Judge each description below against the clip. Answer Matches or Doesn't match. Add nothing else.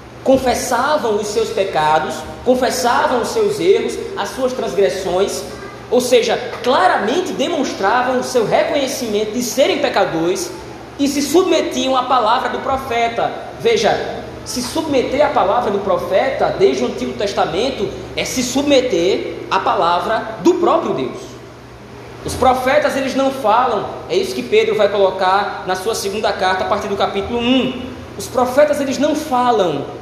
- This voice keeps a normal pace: Matches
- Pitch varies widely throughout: Matches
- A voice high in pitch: Matches